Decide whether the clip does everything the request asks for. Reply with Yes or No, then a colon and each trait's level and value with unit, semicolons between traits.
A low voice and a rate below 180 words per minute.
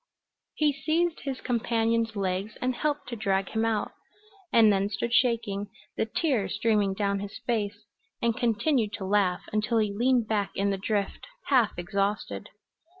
No: high, 220 Hz; average, 155 wpm